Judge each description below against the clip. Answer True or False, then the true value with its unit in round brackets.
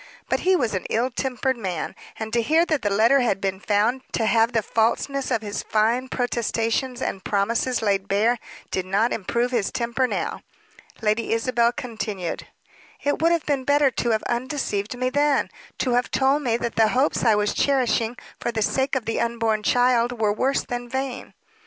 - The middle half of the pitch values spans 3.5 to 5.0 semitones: False (3.1 semitones)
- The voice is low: False (235 Hz)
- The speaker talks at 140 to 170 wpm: False (190 wpm)